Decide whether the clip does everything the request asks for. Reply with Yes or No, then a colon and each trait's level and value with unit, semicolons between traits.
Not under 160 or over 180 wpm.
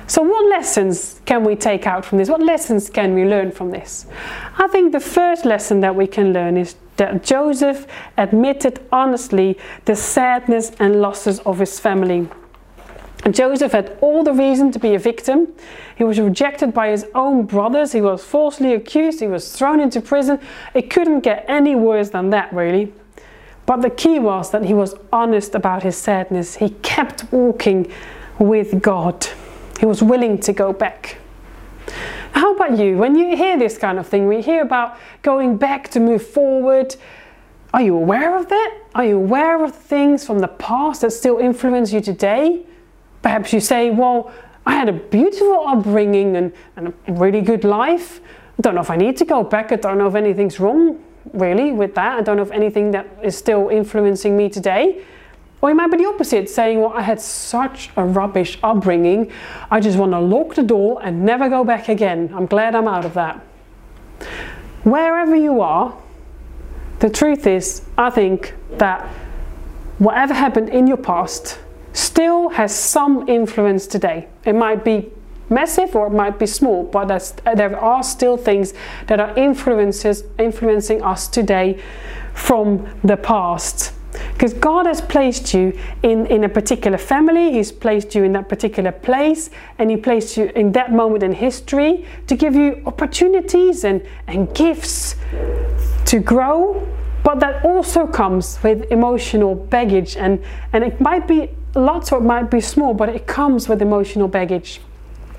Yes: average, 175 wpm